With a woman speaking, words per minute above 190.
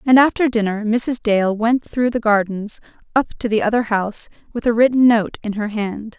Yes: female; fast, 205 wpm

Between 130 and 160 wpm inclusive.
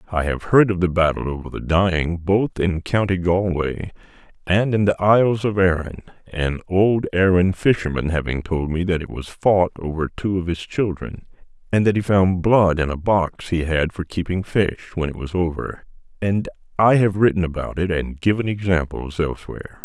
No: average, 190 wpm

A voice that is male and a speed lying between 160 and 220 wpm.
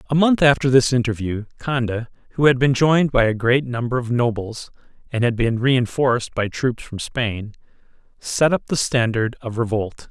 Yes: male; average, 185 wpm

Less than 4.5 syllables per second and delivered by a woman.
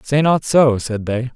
No: 4.0 syllables/s; male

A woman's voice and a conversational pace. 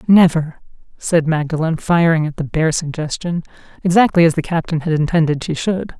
Yes: female; average, 160 wpm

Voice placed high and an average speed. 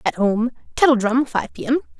Yes: high, 245 Hz; average, 180 wpm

